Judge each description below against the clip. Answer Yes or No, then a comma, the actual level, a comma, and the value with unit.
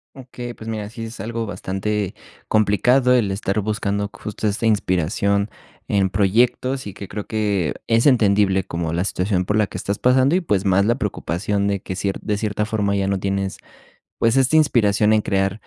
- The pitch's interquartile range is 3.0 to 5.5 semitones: No, narrow, 2.5 semitones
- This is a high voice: No, low, 105 Hz